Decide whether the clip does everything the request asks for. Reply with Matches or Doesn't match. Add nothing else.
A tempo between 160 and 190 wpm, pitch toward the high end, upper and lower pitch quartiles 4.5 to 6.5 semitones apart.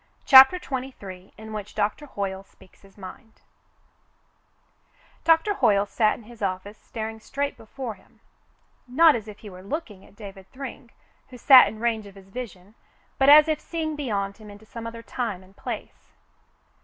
Matches